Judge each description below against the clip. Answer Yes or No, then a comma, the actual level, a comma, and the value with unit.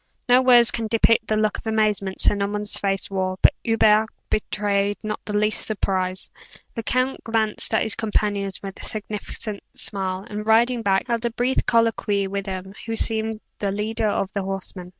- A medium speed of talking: Yes, average, 180 wpm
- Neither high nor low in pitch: No, high, 210 Hz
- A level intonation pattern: Yes, narrow, 2.1 semitones